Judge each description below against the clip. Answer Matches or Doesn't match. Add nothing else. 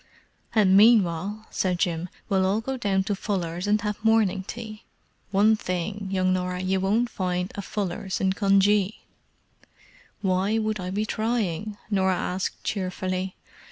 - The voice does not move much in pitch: Matches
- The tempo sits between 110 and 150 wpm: Matches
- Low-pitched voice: Doesn't match